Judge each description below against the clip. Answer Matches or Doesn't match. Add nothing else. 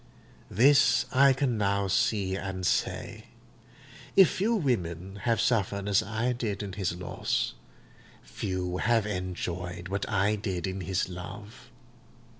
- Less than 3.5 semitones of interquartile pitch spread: Doesn't match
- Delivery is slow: Matches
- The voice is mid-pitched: Doesn't match